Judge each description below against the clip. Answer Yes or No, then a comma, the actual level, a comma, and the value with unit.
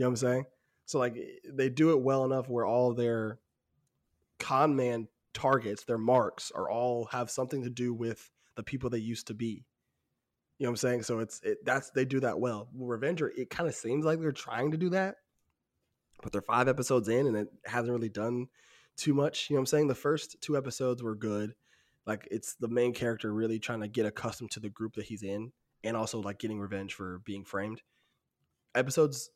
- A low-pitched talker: Yes, low, 120 Hz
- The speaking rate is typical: No, fast, 215 wpm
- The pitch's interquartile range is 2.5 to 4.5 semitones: Yes, average, 2.9 semitones